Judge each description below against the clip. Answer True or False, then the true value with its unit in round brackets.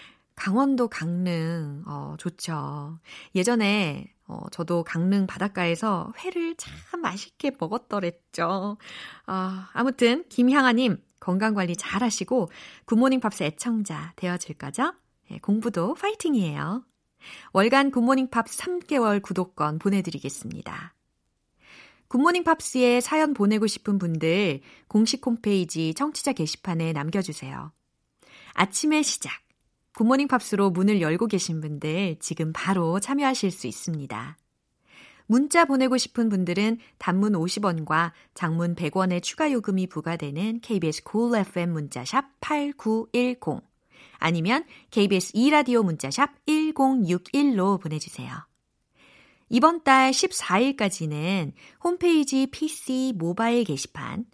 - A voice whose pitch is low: False (205 Hz)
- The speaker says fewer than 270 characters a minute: True (255 characters per minute)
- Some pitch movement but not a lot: False (7.2 semitones)